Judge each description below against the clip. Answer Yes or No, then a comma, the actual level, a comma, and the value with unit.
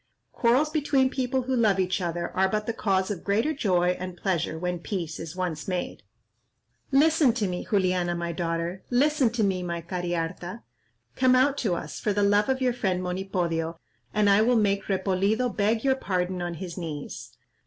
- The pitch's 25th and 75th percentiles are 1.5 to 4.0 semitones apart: No, average, 4.9 semitones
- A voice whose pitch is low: No, high, 190 Hz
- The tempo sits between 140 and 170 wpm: No, average, 185 wpm